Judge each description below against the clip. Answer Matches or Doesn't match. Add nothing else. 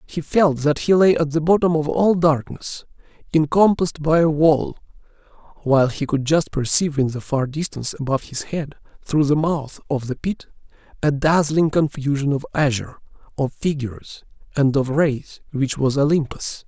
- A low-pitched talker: Doesn't match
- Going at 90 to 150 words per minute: Doesn't match